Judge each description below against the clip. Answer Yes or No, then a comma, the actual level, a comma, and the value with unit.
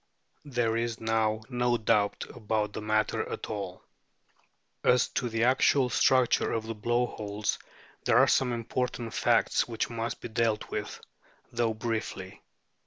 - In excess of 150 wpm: No, average, 145 wpm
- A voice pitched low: Yes, low, 115 Hz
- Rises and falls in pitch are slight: Yes, narrow, 1.9 semitones